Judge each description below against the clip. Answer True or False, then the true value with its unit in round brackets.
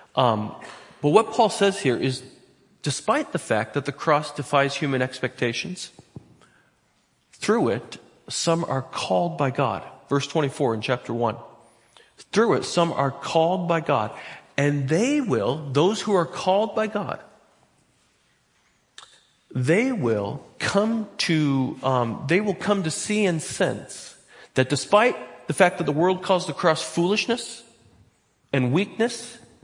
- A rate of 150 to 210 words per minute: False (140 wpm)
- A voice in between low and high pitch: True (155 Hz)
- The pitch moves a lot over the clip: True (6.7 semitones)